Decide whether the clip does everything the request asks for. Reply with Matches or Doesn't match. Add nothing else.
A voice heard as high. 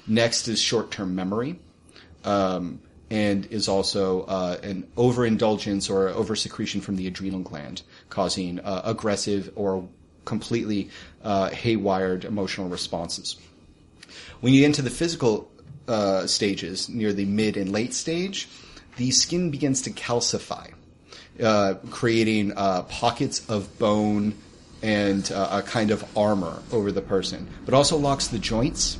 Doesn't match